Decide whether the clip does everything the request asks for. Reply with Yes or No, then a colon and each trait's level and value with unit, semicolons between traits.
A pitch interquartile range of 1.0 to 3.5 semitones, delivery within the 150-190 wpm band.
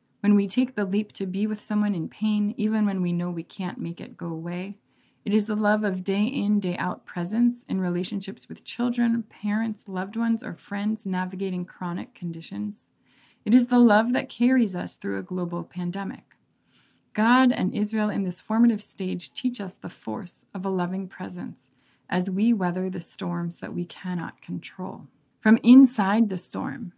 Yes: average, 3.1 semitones; average, 180 wpm